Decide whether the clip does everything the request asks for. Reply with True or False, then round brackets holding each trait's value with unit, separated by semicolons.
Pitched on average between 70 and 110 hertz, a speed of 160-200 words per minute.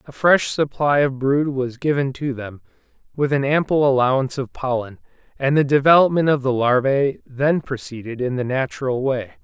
False (135 Hz; 170 wpm)